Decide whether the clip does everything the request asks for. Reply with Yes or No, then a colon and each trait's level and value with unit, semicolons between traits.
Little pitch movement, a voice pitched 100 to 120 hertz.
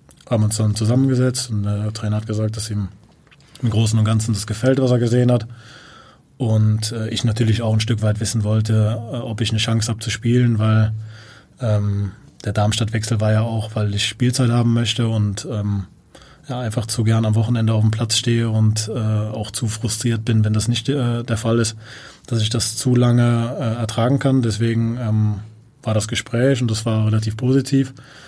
Yes: narrow, 1.7 semitones; low, 115 Hz